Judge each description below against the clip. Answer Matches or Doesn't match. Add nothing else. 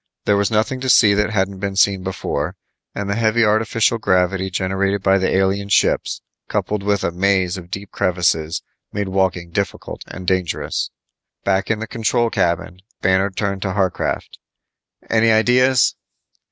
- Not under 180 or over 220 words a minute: Doesn't match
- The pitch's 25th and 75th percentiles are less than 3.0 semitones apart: Matches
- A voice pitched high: Doesn't match